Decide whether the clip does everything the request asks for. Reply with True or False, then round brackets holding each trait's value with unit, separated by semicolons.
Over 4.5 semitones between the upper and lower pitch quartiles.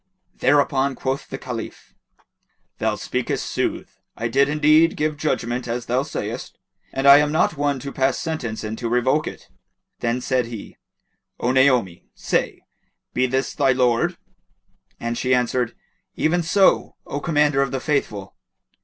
False (3.2 semitones)